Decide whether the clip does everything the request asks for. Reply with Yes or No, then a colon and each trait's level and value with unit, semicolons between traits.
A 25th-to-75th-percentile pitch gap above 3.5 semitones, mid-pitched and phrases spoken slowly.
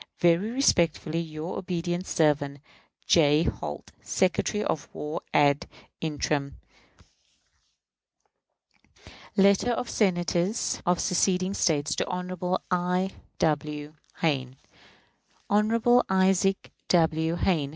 Yes: average, 3.9 semitones; medium, 175 Hz; slow, 90 wpm